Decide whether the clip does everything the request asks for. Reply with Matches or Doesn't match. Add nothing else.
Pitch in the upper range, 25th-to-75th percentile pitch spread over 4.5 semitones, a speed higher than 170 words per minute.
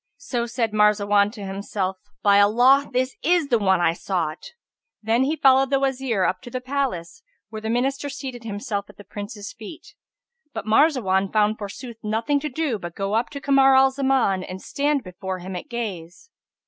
Matches